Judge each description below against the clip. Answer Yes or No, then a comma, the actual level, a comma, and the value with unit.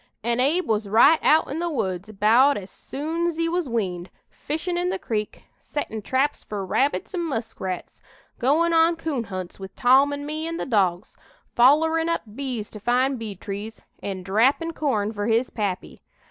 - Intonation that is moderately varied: No, wide, 7.2 semitones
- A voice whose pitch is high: Yes, very high, 255 Hz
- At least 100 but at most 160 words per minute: No, average, 175 wpm